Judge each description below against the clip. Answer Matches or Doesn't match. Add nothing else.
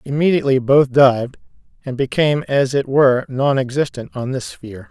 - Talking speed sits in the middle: Matches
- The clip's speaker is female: Doesn't match